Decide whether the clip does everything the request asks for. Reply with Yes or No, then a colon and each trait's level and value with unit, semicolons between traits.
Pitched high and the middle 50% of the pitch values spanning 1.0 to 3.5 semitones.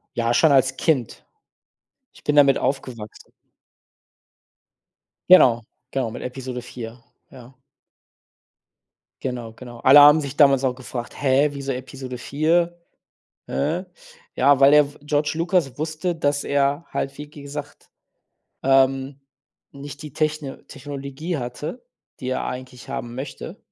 No: medium, 140 Hz; narrow, 2.4 semitones